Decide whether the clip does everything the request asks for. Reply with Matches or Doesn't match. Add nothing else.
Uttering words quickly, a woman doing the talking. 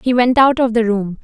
Matches